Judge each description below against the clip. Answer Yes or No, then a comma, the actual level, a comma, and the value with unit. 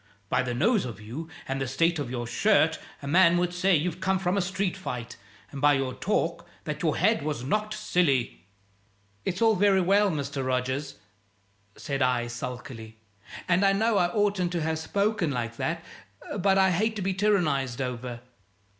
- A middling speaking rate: Yes, average, 180 wpm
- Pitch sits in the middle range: Yes, medium, 165 Hz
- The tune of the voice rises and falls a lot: Yes, wide, 6.6 semitones